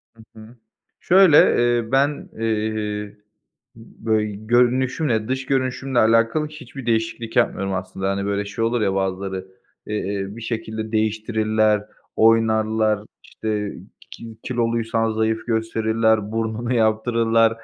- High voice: No, low, 110 Hz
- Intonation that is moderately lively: No, narrow, 1.5 semitones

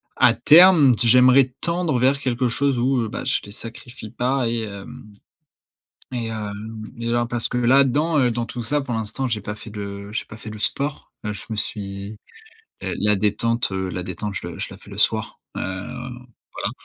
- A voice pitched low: Yes, low, 115 Hz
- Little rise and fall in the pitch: No, average, 3.5 semitones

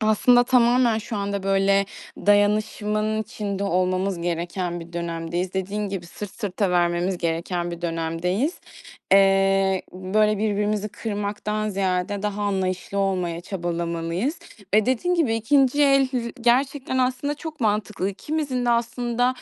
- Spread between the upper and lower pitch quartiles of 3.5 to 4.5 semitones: Yes, average, 4.0 semitones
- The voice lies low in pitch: No, high, 200 Hz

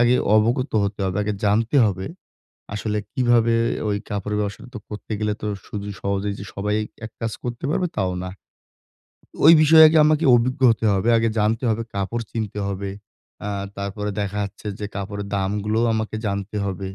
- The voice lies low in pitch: Yes, low, 105 Hz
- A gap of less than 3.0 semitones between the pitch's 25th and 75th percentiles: Yes, narrow, 2.5 semitones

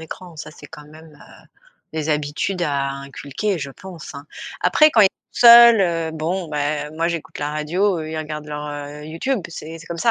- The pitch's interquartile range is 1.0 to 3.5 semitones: Yes, average, 2.9 semitones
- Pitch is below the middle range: No, medium, 155 Hz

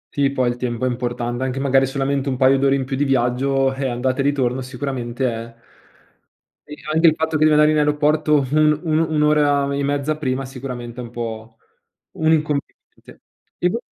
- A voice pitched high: No, low, 135 Hz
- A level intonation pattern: No, average, 3.0 semitones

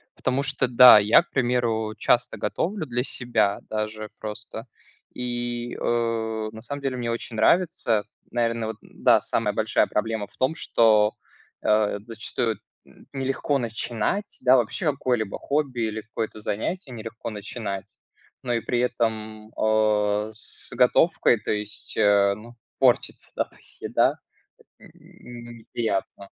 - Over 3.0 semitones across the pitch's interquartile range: No, narrow, 2.4 semitones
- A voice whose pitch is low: Yes, low, 115 Hz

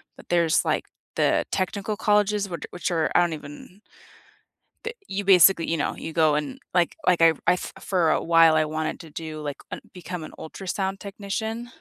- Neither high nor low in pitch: Yes, medium, 175 Hz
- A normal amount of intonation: Yes, average, 3.6 semitones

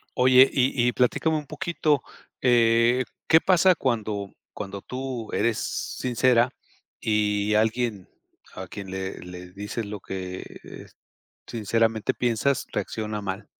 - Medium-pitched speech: No, low, 115 Hz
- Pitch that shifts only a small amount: No, average, 3.8 semitones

